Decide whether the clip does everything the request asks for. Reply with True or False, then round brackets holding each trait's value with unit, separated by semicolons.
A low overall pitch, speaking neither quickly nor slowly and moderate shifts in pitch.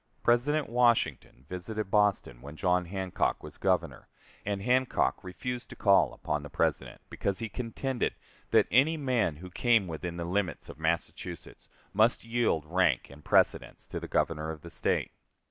False (95 Hz; 160 wpm; 6.2 semitones)